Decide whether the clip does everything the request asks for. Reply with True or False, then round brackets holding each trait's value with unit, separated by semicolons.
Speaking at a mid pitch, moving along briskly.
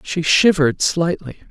False (160 Hz; 120 wpm)